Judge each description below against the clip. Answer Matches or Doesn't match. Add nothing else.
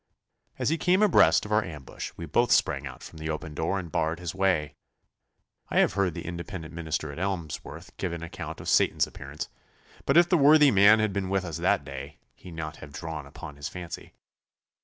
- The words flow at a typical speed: Doesn't match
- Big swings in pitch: Doesn't match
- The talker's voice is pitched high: Doesn't match